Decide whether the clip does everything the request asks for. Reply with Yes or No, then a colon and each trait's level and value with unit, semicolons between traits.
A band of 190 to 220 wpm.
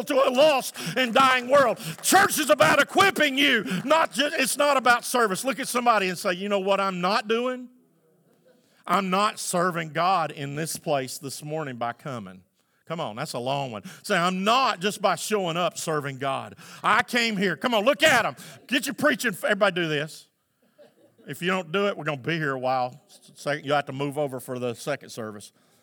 Yes: fast, 205 wpm